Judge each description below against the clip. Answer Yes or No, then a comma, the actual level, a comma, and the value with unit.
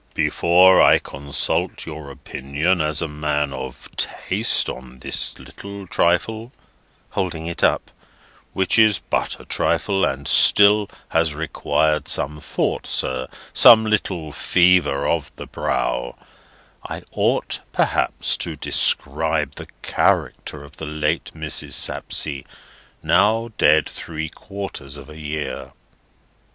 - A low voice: Yes, very low, 80 Hz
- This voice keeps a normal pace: No, slow, 120 wpm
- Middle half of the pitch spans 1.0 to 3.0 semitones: No, average, 4.4 semitones